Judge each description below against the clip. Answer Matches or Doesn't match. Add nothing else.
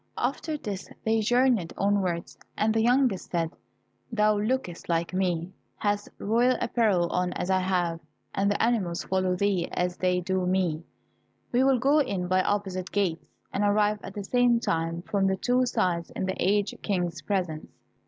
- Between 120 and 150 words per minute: Doesn't match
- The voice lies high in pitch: Matches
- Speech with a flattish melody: Doesn't match